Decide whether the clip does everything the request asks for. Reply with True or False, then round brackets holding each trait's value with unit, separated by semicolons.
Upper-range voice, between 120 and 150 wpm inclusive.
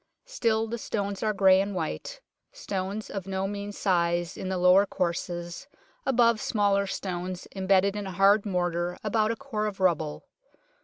False (195 Hz; 160 wpm)